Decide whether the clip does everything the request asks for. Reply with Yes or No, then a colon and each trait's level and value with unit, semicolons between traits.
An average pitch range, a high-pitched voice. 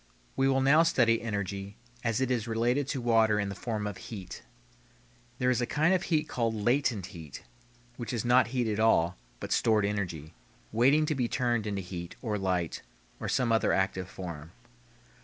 No: average, 4.3 semitones; low, 115 Hz